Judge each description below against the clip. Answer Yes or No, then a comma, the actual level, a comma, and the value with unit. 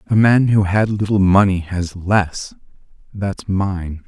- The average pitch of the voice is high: No, very low, 95 Hz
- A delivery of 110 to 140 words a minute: Yes, slow, 135 wpm